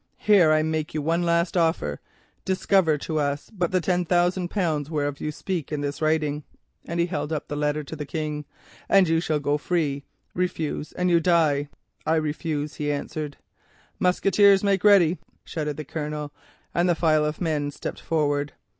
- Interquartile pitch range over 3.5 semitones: No, average, 2.9 semitones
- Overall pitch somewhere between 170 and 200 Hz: No, medium, 155 Hz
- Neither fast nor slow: Yes, average, 175 wpm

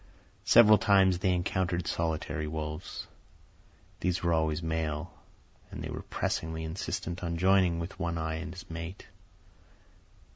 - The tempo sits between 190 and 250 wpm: No, slow, 135 wpm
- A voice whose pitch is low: Yes, very low, 85 Hz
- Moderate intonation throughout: No, narrow, 2.3 semitones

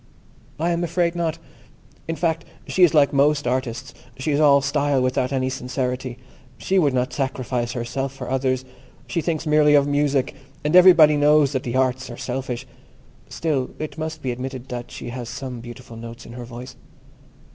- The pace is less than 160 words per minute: No, average, 180 wpm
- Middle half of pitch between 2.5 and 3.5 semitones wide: Yes, average, 3.1 semitones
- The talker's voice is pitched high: No, low, 135 Hz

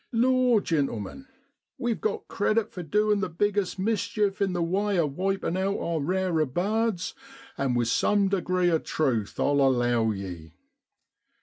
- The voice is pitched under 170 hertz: No, medium, 185 Hz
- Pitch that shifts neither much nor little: No, wide, 6.5 semitones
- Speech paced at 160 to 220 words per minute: No, average, 145 wpm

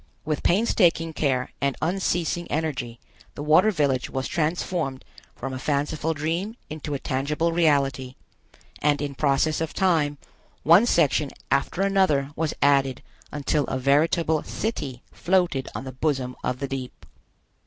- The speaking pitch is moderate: Yes, medium, 150 Hz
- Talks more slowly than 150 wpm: Yes, average, 140 wpm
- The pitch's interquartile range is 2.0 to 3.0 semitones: No, average, 3.4 semitones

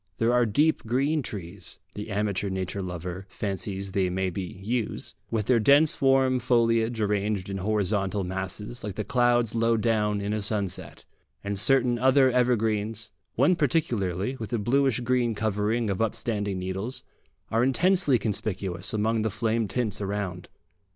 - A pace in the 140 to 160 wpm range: Yes, average, 150 wpm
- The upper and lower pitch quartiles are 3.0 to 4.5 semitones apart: Yes, average, 3.6 semitones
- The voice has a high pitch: No, low, 110 Hz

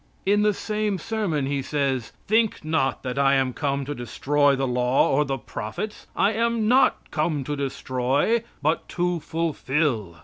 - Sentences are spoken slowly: No, average, 165 wpm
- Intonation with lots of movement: Yes, wide, 6.9 semitones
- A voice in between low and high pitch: Yes, medium, 145 Hz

